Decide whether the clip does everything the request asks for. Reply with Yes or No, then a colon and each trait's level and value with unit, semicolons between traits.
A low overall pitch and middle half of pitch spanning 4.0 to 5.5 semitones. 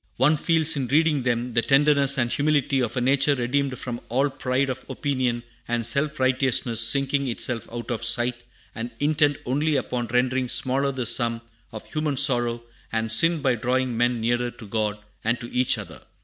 No: low, 130 Hz; average, 2.7 semitones